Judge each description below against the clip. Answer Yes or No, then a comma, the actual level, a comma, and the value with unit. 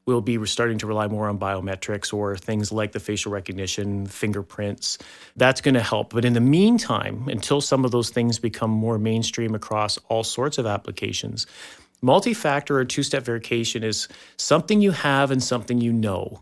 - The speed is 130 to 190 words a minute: Yes, average, 185 wpm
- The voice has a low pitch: Yes, low, 115 Hz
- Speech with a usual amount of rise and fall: Yes, average, 3.3 semitones